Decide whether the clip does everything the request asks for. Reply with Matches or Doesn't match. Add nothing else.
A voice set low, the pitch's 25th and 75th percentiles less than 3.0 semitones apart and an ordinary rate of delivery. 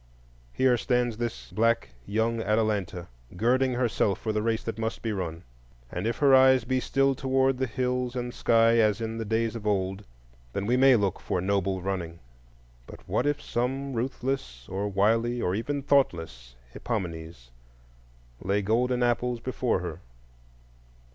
Doesn't match